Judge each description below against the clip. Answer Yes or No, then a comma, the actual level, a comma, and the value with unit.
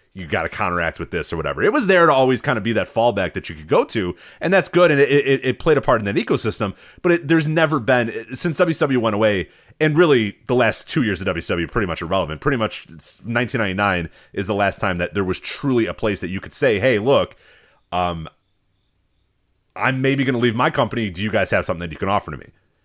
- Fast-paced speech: Yes, fast, 250 wpm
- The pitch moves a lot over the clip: Yes, wide, 6.3 semitones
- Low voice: Yes, low, 110 Hz